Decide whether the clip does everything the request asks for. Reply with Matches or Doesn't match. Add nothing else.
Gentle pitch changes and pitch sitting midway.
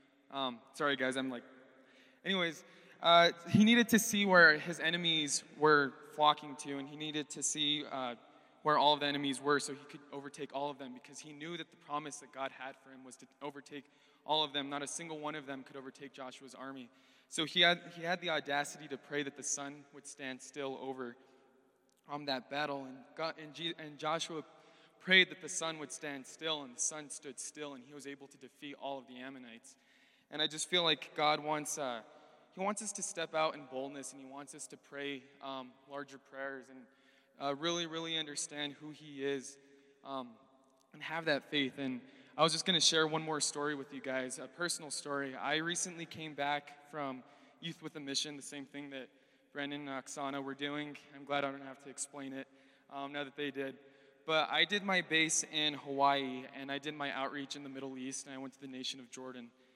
Matches